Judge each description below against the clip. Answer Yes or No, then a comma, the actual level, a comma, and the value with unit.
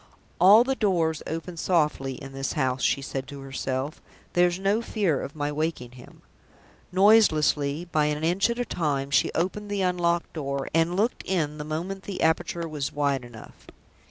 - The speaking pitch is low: No, medium, 160 Hz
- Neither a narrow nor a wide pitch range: Yes, average, 4.6 semitones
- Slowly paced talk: No, average, 175 wpm